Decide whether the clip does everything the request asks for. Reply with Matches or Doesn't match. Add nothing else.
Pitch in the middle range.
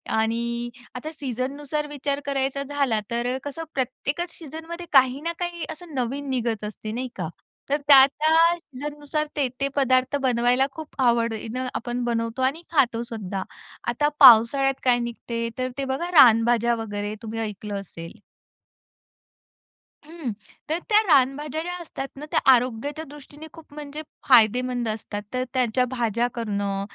Doesn't match